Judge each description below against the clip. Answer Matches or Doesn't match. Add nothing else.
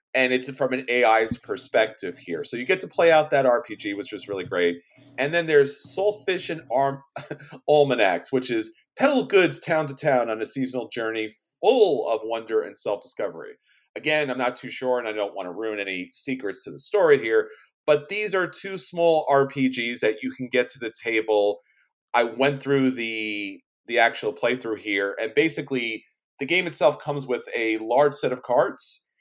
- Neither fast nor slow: Matches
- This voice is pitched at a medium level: Doesn't match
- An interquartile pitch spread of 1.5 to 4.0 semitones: Doesn't match